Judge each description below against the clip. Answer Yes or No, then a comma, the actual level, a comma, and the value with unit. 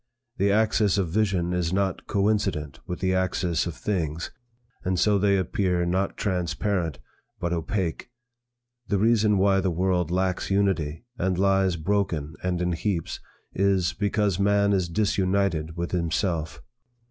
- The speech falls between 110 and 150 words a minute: Yes, average, 140 wpm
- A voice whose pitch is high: No, very low, 95 Hz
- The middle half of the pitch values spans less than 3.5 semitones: Yes, narrow, 2.5 semitones